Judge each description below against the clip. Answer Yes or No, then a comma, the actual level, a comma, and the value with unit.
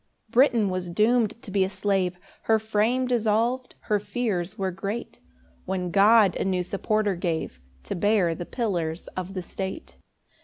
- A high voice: Yes, high, 200 Hz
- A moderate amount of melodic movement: Yes, average, 3.3 semitones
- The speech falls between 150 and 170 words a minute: Yes, average, 160 wpm